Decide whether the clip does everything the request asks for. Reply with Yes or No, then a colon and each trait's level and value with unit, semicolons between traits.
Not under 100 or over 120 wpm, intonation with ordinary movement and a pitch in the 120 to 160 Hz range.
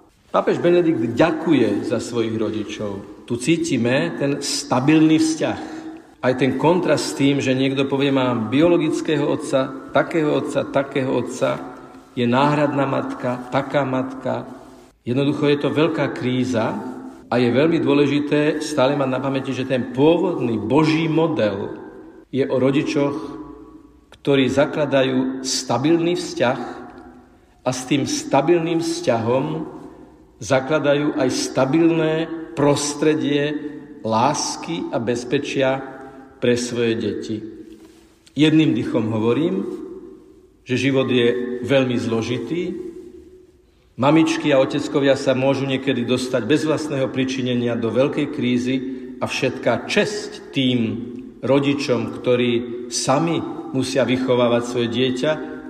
Yes: slow, 110 wpm; average, 3.6 semitones; low, 135 Hz